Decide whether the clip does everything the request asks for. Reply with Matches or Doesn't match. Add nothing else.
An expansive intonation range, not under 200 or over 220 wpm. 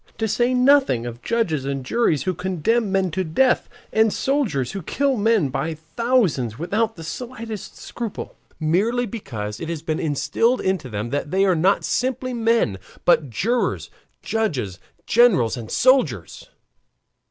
Doesn't match